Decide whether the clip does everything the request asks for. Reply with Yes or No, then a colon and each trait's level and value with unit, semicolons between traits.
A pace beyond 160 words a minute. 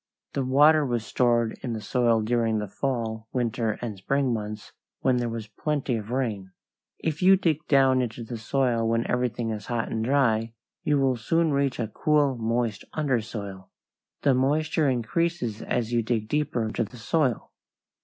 Yes: average, 170 wpm